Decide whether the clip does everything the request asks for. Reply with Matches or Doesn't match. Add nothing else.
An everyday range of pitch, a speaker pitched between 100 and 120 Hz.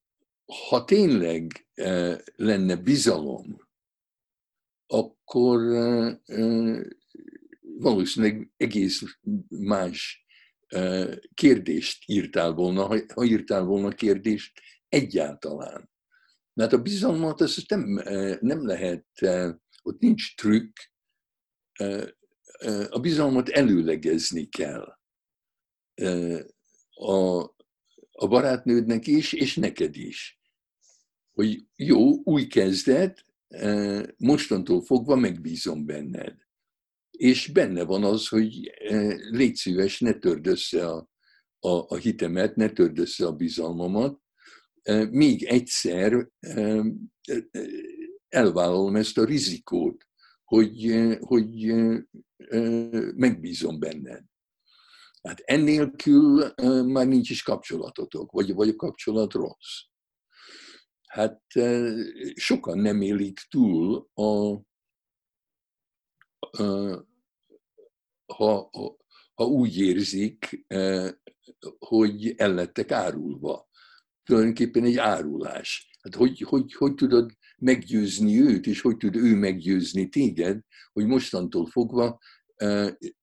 Doesn't match